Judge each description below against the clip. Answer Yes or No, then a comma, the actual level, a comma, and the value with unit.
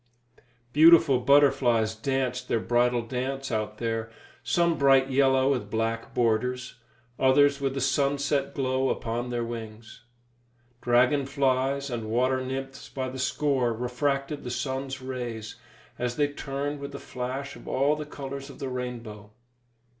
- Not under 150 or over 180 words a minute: No, average, 140 wpm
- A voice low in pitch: Yes, low, 130 Hz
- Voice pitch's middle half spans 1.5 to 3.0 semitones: Yes, narrow, 2.4 semitones